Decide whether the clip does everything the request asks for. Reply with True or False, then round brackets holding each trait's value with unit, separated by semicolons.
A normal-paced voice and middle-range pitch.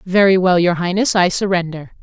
True (180 wpm; 180 Hz)